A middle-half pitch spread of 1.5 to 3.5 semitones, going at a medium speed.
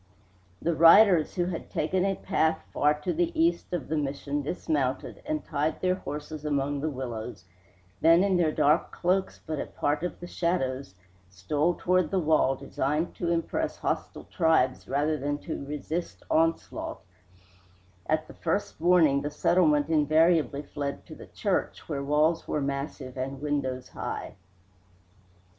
Yes: average, 3.2 semitones; average, 150 wpm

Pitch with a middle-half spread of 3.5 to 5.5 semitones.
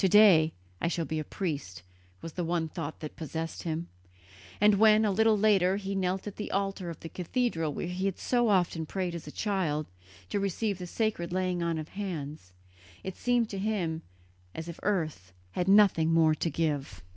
Yes: average, 3.8 semitones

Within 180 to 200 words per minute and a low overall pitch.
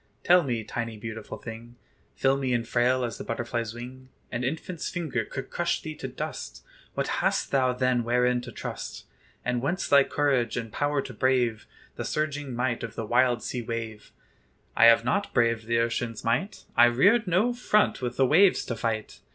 Yes: average, 185 wpm; low, 125 Hz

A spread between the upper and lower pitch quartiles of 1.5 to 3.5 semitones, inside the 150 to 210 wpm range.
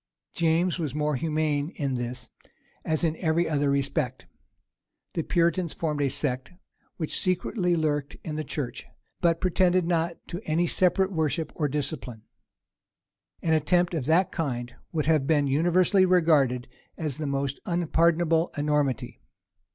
No: average, 3.1 semitones; average, 140 wpm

